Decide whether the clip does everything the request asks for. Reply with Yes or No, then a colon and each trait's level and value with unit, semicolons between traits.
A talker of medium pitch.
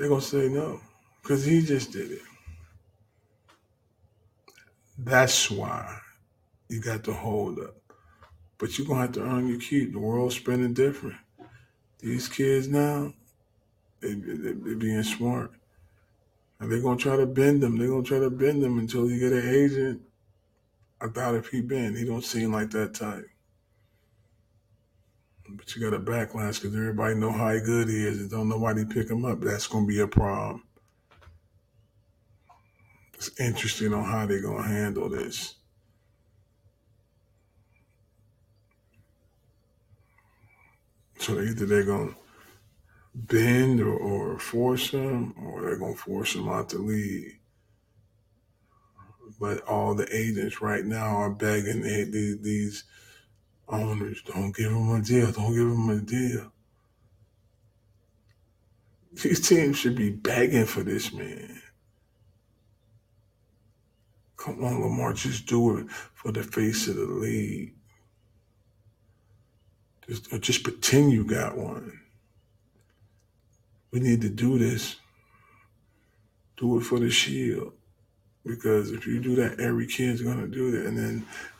No: low, 110 Hz